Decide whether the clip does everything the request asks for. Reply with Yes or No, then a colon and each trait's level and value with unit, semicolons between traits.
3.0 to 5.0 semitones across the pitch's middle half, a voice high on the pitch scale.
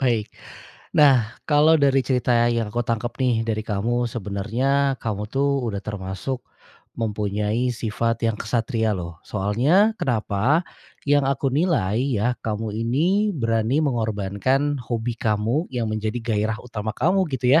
No: average, 4.1 semitones; low, 115 Hz